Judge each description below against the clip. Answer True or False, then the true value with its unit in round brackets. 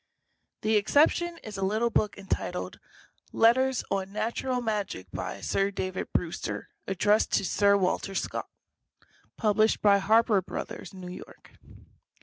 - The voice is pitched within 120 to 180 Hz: False (205 Hz)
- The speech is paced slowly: True (130 wpm)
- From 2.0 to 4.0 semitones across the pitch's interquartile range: True (2.6 semitones)